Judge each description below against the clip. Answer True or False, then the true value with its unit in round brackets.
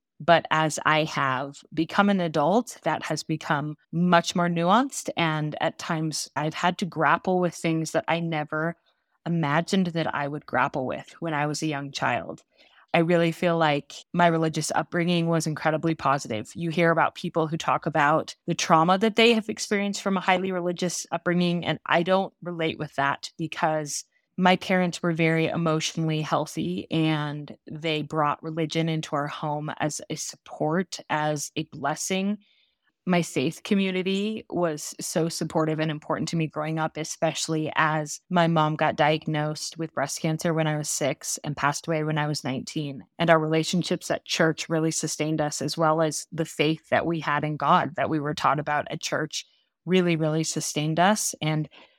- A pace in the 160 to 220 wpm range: True (175 wpm)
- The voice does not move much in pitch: True (2.1 semitones)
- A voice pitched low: False (160 Hz)